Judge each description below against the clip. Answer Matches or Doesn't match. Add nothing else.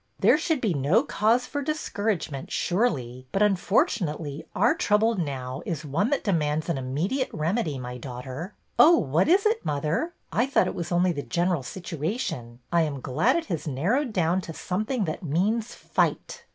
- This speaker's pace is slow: Doesn't match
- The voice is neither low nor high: Matches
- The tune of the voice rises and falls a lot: Matches